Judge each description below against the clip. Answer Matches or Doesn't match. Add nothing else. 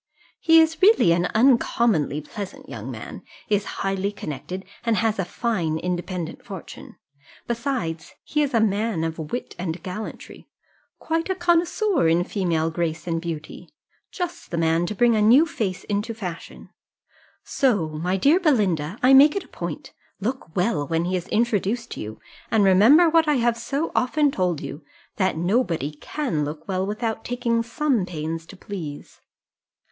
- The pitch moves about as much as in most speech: Doesn't match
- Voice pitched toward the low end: Doesn't match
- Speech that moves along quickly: Doesn't match